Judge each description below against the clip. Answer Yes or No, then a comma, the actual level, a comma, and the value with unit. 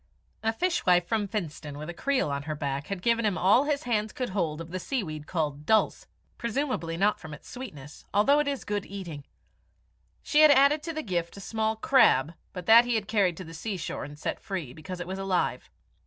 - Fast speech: Yes, fast, 215 wpm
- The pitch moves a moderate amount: No, wide, 6.3 semitones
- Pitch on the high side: Yes, high, 195 Hz